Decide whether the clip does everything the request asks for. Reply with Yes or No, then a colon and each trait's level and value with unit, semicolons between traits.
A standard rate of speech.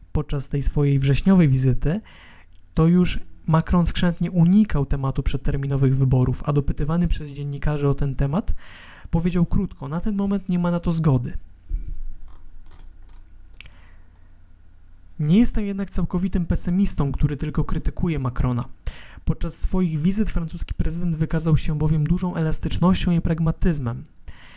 Yes: average, 125 wpm